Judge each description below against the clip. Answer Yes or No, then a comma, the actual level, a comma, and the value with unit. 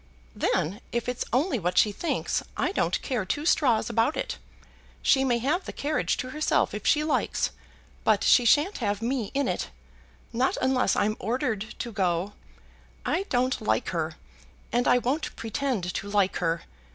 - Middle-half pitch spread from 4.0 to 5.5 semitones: Yes, average, 4.9 semitones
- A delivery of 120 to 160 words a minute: No, average, 170 wpm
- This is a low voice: No, high, 245 Hz